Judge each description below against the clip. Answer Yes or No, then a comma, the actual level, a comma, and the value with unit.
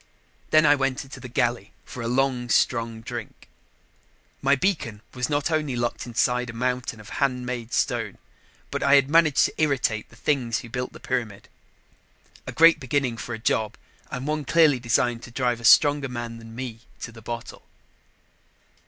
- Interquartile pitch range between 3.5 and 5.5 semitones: No, average, 3.0 semitones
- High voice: No, low, 125 Hz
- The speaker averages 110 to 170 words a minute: No, average, 180 wpm